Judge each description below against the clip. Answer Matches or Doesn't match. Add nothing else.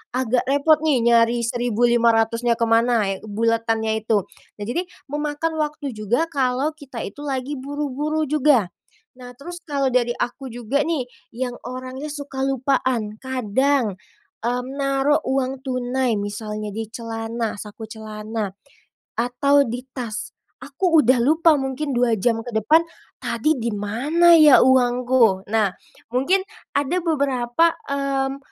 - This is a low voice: Doesn't match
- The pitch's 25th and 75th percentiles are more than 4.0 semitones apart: Doesn't match